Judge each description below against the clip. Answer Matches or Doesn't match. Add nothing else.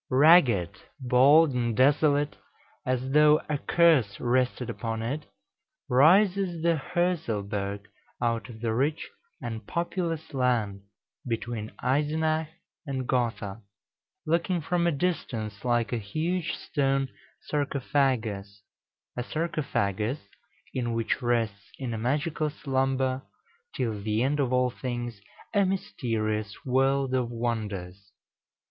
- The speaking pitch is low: Matches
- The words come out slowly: Matches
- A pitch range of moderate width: Matches